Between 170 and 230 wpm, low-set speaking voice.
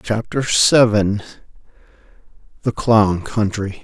No: slow, 80 wpm; low, 110 Hz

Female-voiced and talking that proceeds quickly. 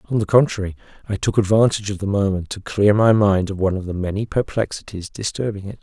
No: male; fast, 215 wpm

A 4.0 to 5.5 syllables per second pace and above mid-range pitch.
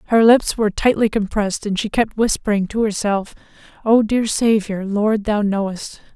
Yes: 4.9 syllables/s; high, 210 Hz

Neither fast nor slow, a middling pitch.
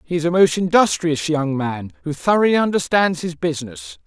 Yes: average, 175 wpm; medium, 155 Hz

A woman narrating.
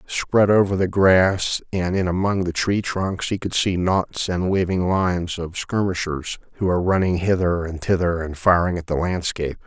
No: male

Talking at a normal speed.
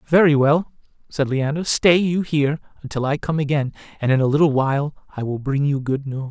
No: fast, 210 wpm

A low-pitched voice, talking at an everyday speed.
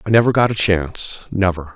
Yes: very low, 95 Hz; average, 170 wpm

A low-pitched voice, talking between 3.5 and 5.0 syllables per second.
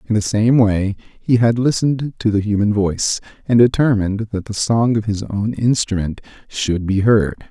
Yes: low, 110 Hz; 4.8 syllables/s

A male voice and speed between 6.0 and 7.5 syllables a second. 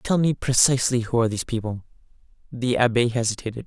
Yes: male; 6.7 syllables/s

